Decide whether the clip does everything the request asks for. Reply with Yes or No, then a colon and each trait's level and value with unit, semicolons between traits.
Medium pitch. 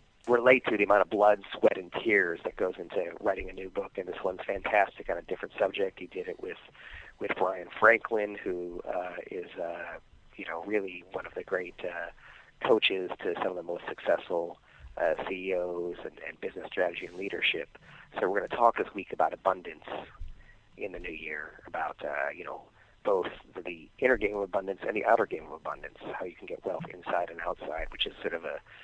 No: low, 105 Hz